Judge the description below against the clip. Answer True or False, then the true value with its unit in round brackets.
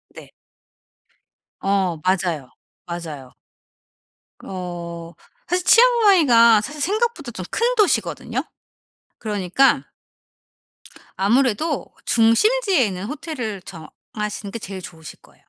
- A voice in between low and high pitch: False (215 Hz)